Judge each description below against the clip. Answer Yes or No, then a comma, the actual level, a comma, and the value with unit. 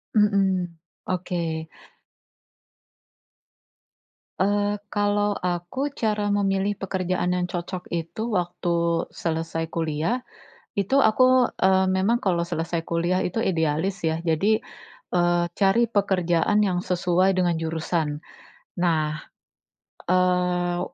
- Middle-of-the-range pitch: Yes, medium, 180 Hz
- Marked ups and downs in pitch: No, average, 2.7 semitones